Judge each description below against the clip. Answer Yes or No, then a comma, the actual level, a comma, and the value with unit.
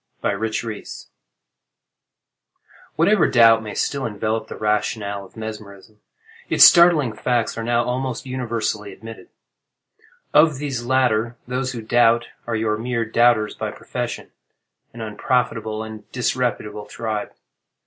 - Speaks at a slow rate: Yes, slow, 120 wpm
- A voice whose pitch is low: Yes, low, 115 Hz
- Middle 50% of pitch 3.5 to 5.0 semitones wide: No, narrow, 2.5 semitones